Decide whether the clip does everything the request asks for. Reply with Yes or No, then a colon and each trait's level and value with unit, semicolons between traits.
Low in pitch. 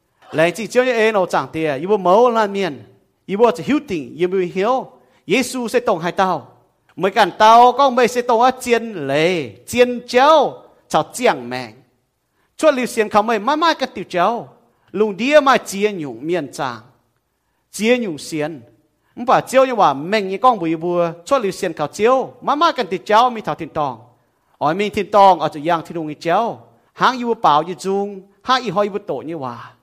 No: high, 195 Hz